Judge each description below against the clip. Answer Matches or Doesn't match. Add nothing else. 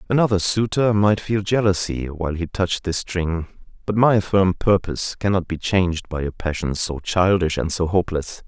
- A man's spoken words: Matches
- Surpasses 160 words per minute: Matches